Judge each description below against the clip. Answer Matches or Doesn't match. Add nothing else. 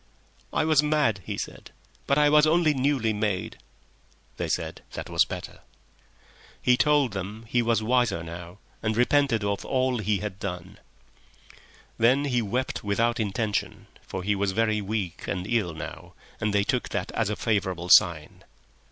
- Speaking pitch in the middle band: Doesn't match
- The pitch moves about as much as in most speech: Matches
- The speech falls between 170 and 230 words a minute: Doesn't match